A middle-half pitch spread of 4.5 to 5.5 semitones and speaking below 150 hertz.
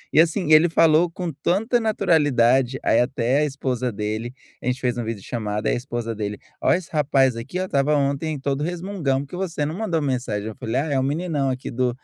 Yes: average, 4.8 semitones; low, 135 Hz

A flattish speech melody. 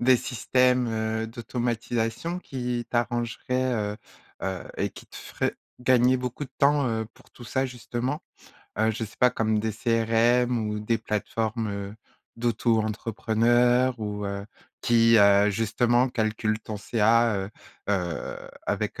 Yes: narrow, 2.2 semitones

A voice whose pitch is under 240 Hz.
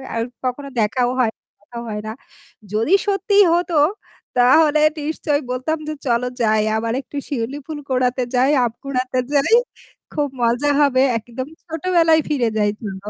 No: very high, 255 Hz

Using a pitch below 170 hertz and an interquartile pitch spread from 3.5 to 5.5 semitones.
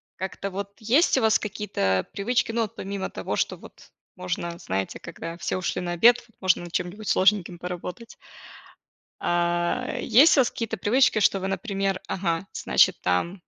No: high, 195 Hz; average, 3.8 semitones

